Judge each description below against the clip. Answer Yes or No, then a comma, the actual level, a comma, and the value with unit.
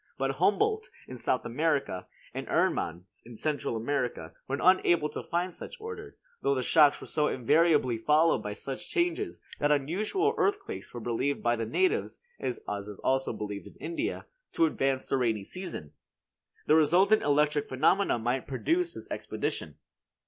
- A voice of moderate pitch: Yes, medium, 145 Hz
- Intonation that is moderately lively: No, wide, 8.0 semitones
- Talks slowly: No, average, 155 wpm